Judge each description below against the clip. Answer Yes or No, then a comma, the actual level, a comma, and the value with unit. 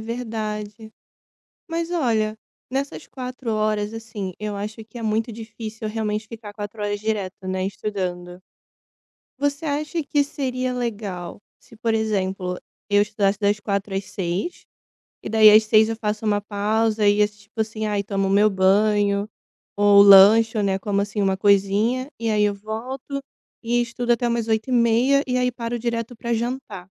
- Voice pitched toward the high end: Yes, high, 215 Hz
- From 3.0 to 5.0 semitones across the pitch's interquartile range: No, narrow, 2.4 semitones